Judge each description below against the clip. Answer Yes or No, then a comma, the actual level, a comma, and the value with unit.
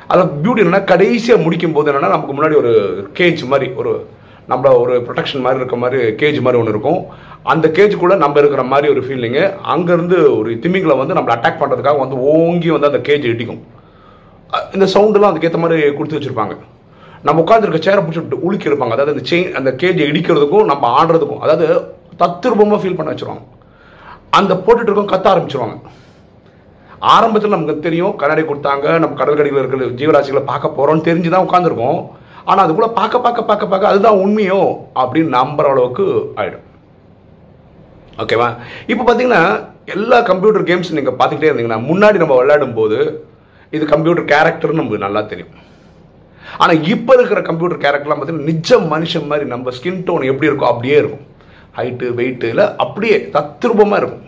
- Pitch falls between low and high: Yes, medium, 170 Hz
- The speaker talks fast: Yes, fast, 155 wpm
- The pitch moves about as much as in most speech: No, wide, 6.3 semitones